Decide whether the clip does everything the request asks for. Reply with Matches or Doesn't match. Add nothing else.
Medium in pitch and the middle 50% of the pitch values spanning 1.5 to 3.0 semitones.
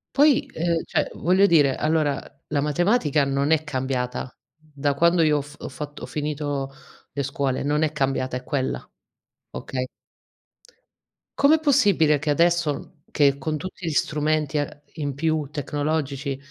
Matches